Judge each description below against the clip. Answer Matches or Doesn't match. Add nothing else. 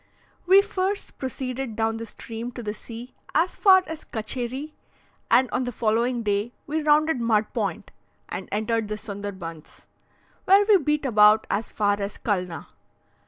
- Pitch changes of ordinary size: Doesn't match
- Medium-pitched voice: Doesn't match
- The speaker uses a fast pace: Doesn't match